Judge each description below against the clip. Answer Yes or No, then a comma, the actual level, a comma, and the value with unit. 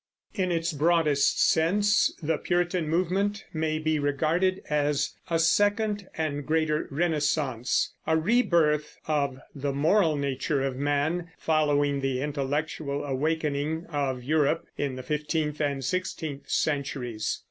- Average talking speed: No, slow, 125 wpm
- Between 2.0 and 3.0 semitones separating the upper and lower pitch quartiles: Yes, narrow, 2.6 semitones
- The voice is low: No, medium, 150 Hz